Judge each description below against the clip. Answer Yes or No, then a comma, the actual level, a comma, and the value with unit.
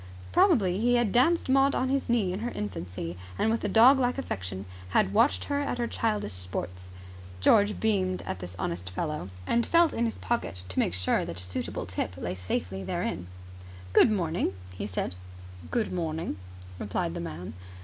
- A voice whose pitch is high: No, medium, 180 Hz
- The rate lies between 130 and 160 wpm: No, average, 180 wpm